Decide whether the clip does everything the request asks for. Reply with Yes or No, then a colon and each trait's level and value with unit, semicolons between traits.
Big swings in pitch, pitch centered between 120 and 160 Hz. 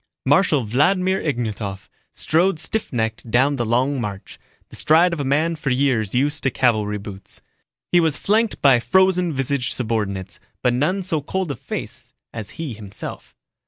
Yes: wide, 6.5 semitones; low, 135 Hz